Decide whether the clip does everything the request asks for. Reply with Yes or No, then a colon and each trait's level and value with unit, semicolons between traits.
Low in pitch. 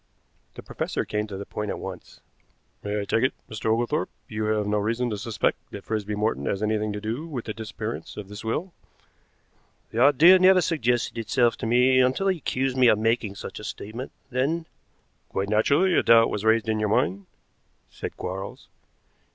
Yes: low, 110 Hz